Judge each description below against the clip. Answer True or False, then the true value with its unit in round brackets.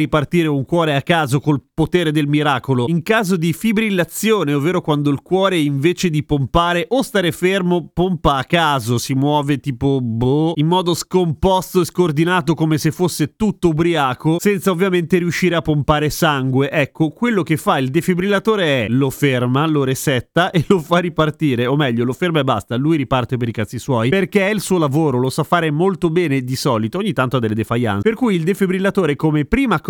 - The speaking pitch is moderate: True (160 Hz)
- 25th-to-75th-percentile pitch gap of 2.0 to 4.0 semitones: False (4.4 semitones)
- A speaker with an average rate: False (195 wpm)